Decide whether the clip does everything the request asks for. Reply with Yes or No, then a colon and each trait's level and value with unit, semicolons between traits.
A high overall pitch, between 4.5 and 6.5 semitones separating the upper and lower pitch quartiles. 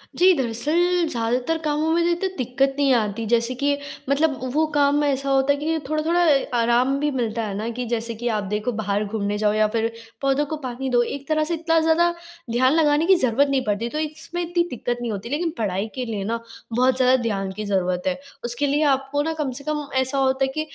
Yes: very high, 265 Hz; average, 4.8 semitones